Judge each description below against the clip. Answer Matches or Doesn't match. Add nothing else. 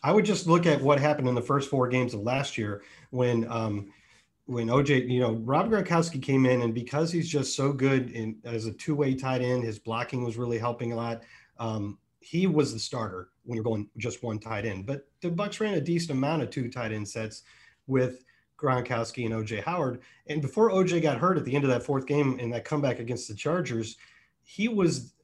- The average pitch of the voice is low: Matches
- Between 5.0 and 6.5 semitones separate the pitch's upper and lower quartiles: Doesn't match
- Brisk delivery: Matches